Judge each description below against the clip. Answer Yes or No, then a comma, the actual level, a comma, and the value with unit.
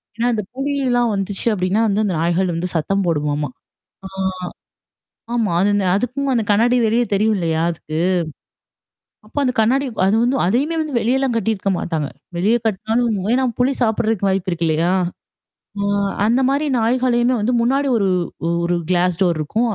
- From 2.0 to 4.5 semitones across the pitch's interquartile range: No, average, 5.1 semitones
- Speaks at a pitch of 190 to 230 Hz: Yes, high, 215 Hz